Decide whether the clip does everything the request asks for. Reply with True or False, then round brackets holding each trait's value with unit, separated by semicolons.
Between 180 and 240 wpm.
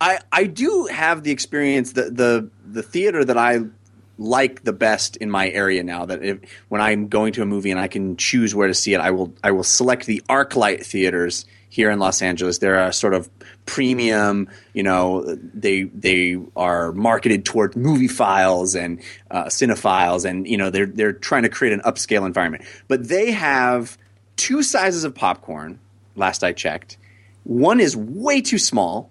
True (185 wpm)